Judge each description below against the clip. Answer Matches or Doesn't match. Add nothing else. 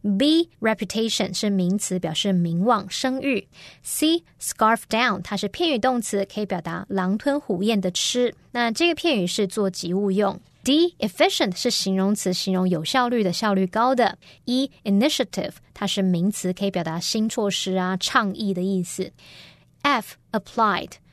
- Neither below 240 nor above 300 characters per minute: Doesn't match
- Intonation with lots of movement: Doesn't match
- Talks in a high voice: Matches